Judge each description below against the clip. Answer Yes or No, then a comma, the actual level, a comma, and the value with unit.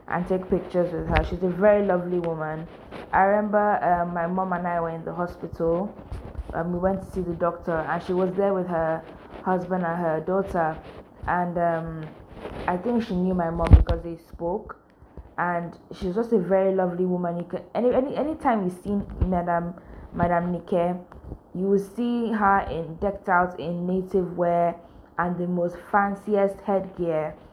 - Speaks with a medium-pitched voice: Yes, medium, 180 Hz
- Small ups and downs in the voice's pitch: Yes, narrow, 2.2 semitones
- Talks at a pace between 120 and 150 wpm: No, average, 180 wpm